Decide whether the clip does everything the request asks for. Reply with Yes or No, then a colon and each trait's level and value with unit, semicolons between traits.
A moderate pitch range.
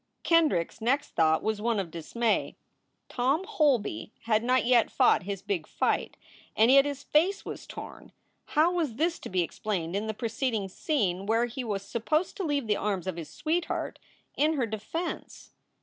No: wide, 6.5 semitones